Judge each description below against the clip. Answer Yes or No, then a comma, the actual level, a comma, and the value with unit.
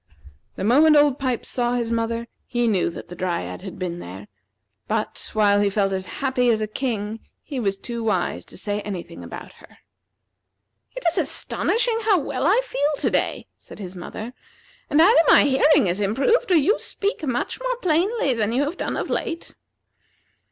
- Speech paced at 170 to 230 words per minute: Yes, average, 185 wpm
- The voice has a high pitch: Yes, high, 240 Hz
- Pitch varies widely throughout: Yes, wide, 6.9 semitones